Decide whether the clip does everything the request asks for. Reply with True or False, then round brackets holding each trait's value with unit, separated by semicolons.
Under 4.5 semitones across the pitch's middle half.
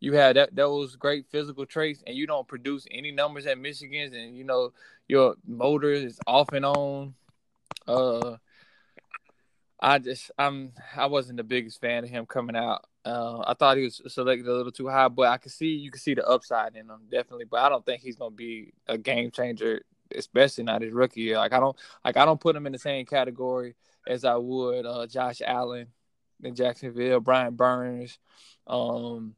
True (2.8 semitones)